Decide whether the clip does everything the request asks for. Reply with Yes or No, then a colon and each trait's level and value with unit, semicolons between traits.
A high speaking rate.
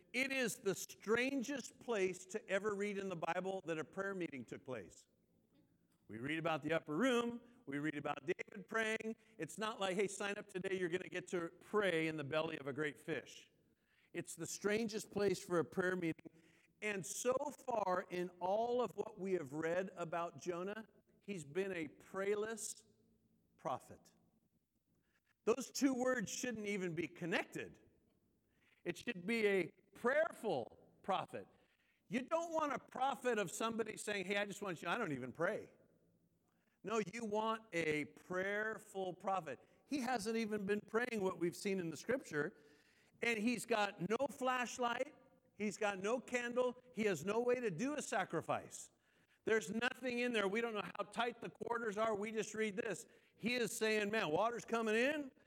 No: average, 175 wpm